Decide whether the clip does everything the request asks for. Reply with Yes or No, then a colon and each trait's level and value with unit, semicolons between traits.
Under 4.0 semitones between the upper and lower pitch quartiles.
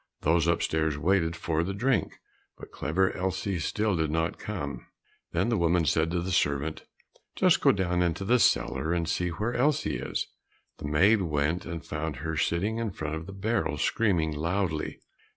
Yes: average, 3.6 semitones